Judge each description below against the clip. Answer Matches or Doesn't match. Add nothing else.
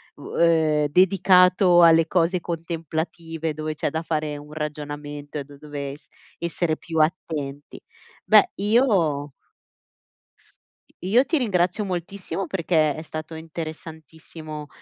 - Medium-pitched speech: Matches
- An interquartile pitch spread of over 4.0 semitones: Doesn't match